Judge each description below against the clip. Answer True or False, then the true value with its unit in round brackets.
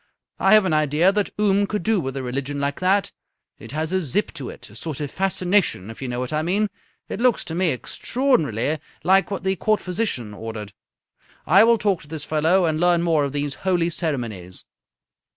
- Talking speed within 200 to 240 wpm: True (205 wpm)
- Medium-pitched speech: True (165 Hz)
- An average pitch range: False (5.7 semitones)